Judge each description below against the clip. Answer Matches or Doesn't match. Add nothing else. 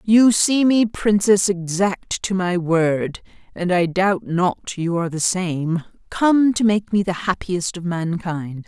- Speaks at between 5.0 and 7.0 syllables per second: Doesn't match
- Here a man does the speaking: Doesn't match